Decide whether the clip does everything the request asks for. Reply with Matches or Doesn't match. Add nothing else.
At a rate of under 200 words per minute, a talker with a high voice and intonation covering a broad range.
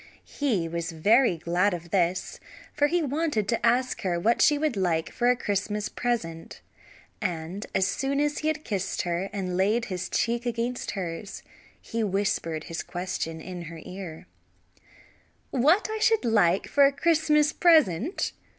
Matches